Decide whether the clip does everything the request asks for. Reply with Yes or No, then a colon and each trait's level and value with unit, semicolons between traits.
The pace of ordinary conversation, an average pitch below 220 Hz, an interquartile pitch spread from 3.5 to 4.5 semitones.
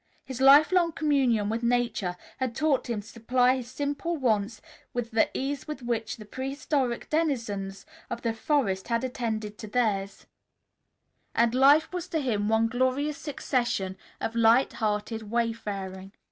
No: average, 150 wpm; high, 240 Hz; average, 3.8 semitones